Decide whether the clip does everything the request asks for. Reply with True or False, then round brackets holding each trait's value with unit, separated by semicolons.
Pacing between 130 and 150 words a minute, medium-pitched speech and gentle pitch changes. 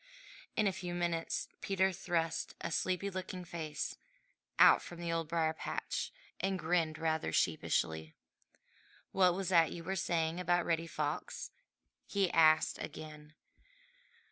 True (135 wpm; 170 Hz; 2.3 semitones)